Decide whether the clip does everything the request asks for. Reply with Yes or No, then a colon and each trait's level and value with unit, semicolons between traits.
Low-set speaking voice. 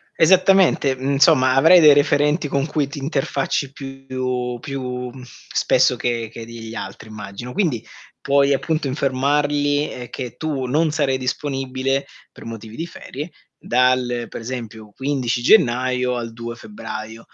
Yes: low, 130 Hz